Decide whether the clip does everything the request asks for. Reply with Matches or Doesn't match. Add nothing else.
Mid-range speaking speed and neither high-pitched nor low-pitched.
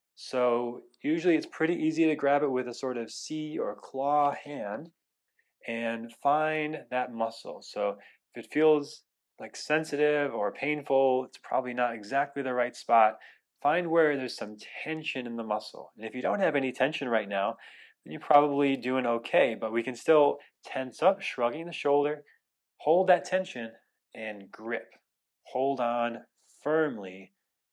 Doesn't match